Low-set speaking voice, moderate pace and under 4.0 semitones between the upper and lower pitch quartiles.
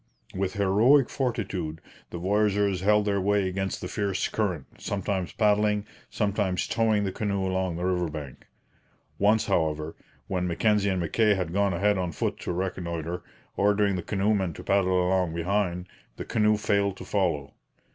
Yes: very low, 95 Hz; average, 155 wpm; narrow, 2.4 semitones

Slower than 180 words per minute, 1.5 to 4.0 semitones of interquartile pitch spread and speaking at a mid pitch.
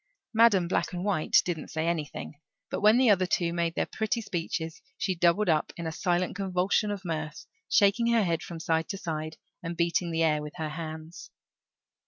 No: average, 195 wpm; average, 3.4 semitones; medium, 170 Hz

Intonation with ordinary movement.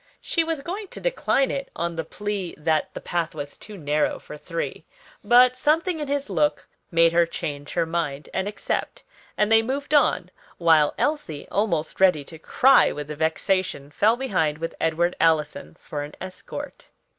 No: wide, 8.1 semitones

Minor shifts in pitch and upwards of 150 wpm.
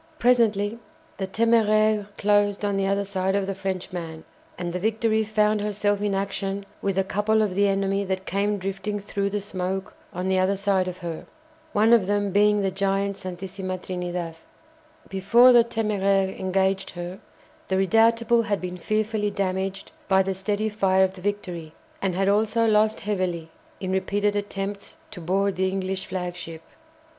Yes: narrow, 1.7 semitones; average, 165 wpm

